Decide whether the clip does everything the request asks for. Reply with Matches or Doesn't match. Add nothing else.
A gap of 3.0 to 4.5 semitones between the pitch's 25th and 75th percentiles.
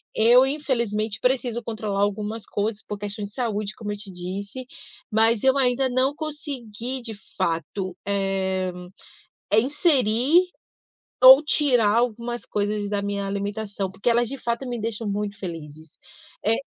Matches